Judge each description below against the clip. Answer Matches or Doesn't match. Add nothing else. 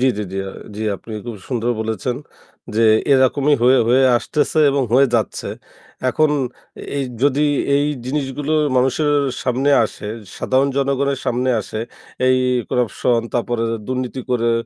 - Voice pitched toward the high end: Doesn't match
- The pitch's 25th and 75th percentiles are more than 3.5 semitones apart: Doesn't match